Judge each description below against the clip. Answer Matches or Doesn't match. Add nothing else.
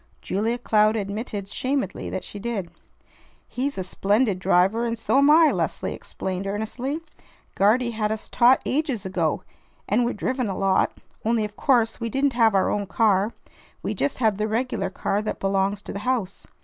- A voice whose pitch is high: Matches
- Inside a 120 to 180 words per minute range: Matches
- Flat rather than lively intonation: Doesn't match